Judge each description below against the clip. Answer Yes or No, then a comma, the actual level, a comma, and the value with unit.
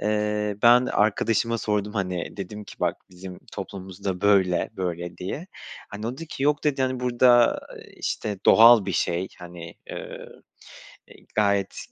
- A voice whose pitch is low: Yes, low, 105 Hz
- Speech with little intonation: No, average, 4.0 semitones